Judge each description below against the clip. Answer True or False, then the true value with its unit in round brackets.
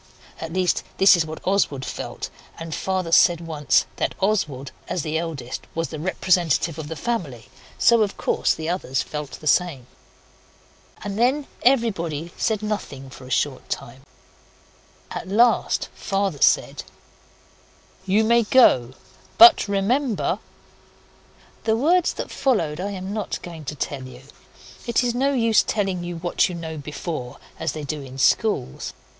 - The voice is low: False (175 Hz)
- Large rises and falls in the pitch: True (6.1 semitones)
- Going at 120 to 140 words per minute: False (155 wpm)